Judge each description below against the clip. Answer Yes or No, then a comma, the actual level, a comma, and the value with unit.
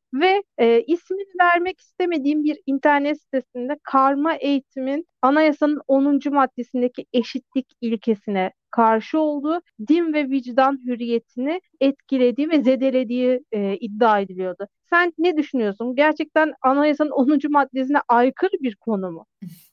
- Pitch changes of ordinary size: Yes, average, 3.8 semitones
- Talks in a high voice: Yes, very high, 270 Hz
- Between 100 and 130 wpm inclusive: Yes, average, 115 wpm